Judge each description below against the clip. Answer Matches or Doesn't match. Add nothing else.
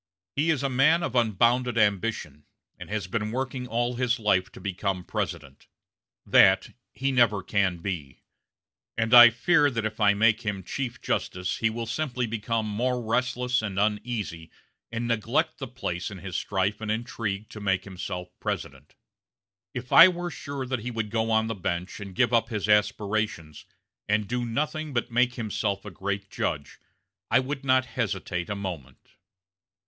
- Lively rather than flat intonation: Doesn't match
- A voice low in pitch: Matches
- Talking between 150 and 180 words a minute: Matches